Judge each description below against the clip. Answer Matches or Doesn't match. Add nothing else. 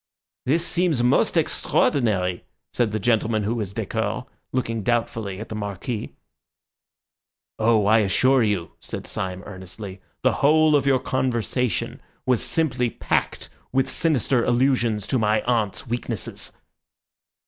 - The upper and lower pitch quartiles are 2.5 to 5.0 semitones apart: Matches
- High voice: Doesn't match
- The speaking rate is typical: Doesn't match